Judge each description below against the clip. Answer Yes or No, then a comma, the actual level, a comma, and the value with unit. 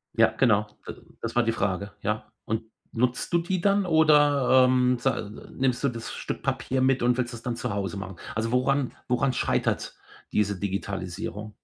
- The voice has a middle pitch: No, low, 120 Hz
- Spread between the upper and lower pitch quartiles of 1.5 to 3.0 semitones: No, average, 3.9 semitones